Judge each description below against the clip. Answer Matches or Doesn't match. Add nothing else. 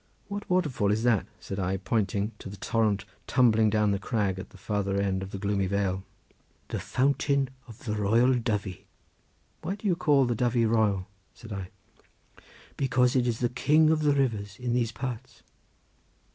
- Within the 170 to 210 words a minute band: Matches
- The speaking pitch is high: Doesn't match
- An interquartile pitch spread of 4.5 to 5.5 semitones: Doesn't match